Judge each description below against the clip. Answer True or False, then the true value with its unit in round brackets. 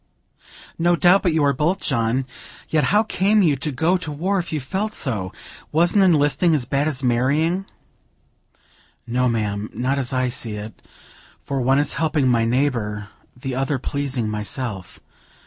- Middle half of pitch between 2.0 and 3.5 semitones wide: False (5.1 semitones)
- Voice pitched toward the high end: False (140 Hz)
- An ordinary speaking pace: True (165 wpm)